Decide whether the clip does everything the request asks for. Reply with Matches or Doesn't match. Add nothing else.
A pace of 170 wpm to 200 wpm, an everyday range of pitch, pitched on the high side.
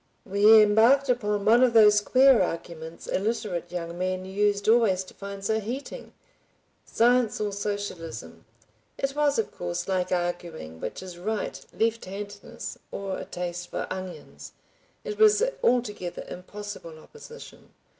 Doesn't match